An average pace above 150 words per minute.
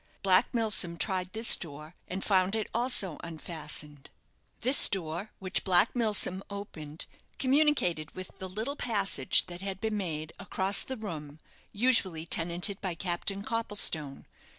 No: slow, 135 wpm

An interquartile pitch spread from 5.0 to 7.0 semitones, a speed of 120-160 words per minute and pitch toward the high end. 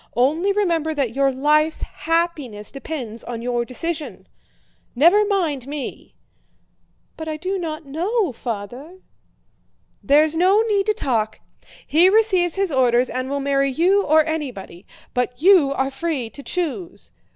Yes: average, 5.3 semitones; average, 140 wpm; very high, 305 Hz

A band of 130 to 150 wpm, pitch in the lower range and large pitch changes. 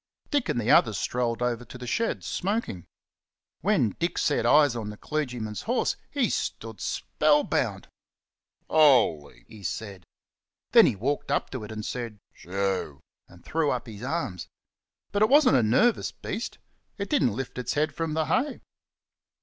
No: average, 165 wpm; low, 125 Hz; wide, 6.7 semitones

